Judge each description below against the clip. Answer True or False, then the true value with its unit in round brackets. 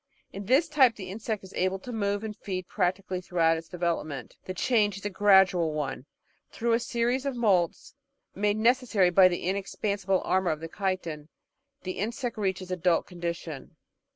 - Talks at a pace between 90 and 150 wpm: False (175 wpm)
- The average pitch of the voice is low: False (190 Hz)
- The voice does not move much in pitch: False (3.4 semitones)